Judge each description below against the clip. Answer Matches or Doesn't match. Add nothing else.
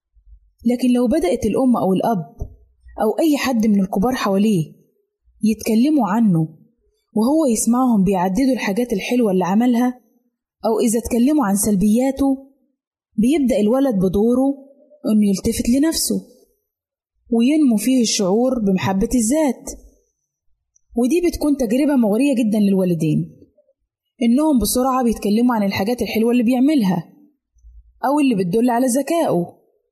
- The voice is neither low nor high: Doesn't match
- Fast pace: Doesn't match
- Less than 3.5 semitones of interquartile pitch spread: Doesn't match